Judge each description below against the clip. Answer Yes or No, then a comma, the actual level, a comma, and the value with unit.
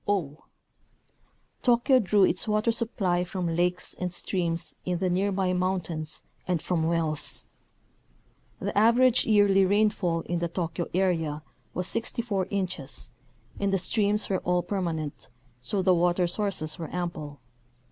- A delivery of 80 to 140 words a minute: Yes, slow, 135 wpm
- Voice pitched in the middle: Yes, medium, 180 Hz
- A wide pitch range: No, average, 3.1 semitones